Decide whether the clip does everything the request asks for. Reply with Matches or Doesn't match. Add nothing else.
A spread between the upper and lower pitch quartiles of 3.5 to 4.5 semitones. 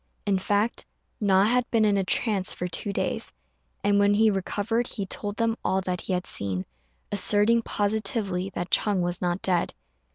Doesn't match